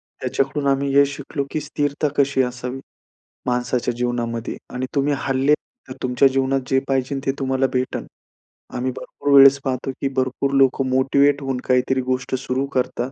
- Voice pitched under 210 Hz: Yes, low, 135 Hz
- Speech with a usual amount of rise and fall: No, narrow, 1.5 semitones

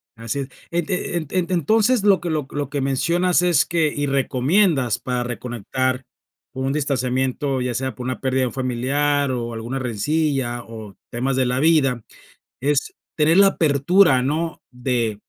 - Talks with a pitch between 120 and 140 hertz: Yes, low, 135 Hz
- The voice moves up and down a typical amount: Yes, average, 3.9 semitones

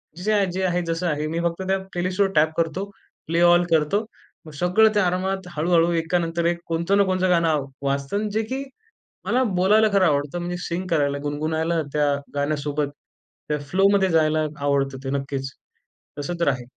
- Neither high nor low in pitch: Yes, medium, 170 Hz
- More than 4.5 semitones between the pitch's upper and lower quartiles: No, average, 3.7 semitones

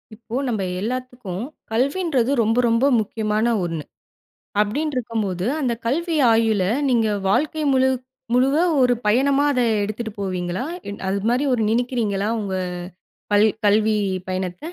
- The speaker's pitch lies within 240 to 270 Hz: No, high, 225 Hz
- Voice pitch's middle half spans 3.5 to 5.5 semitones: Yes, average, 3.8 semitones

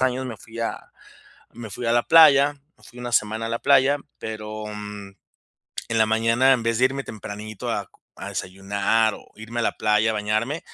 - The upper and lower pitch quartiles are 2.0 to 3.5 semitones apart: Yes, narrow, 2.5 semitones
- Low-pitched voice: Yes, low, 115 Hz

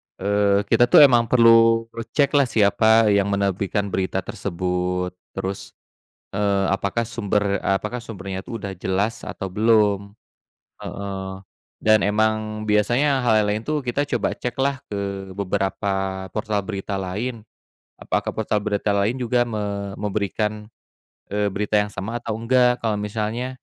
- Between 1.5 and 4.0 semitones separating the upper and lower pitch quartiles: Yes, narrow, 2.5 semitones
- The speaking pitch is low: Yes, low, 105 Hz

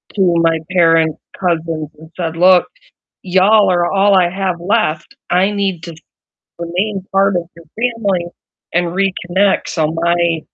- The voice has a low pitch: No, medium, 180 Hz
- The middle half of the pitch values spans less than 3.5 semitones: Yes, narrow, 2.6 semitones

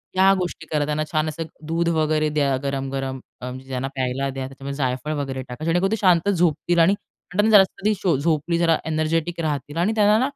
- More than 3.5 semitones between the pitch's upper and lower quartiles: Yes, average, 4.1 semitones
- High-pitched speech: No, medium, 155 Hz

